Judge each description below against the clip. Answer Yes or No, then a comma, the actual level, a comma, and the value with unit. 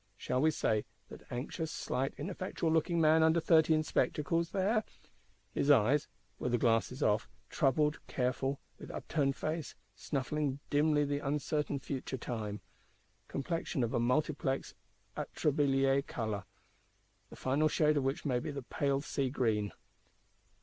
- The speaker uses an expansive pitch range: No, average, 3.3 semitones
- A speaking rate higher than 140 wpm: No, slow, 135 wpm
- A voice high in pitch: No, medium, 140 Hz